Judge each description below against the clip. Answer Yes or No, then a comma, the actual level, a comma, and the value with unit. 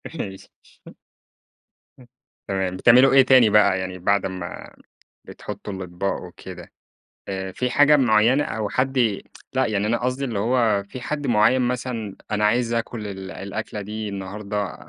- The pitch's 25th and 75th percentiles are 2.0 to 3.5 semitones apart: No, average, 4.1 semitones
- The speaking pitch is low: Yes, low, 105 Hz